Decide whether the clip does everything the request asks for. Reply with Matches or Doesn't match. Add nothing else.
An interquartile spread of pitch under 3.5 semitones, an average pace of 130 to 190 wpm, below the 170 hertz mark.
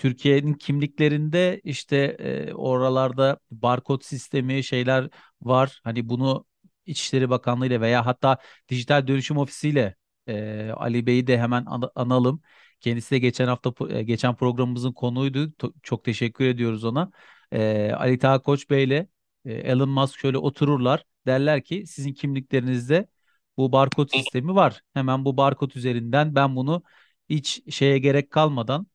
Matches